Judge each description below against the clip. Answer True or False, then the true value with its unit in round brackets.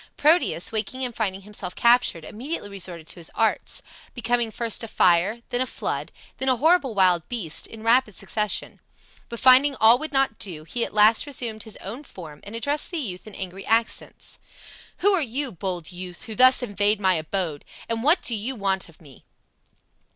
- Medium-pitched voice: False (220 Hz)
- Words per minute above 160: True (190 wpm)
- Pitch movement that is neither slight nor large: True (5.0 semitones)